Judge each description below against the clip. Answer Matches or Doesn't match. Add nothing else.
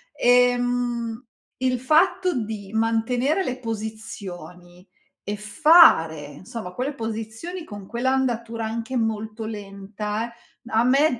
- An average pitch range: Matches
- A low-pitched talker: Doesn't match